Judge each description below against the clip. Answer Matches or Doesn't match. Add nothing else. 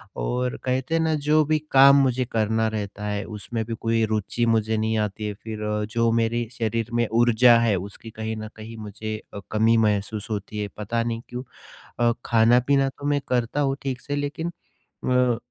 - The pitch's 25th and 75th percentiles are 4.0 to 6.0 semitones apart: Doesn't match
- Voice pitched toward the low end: Matches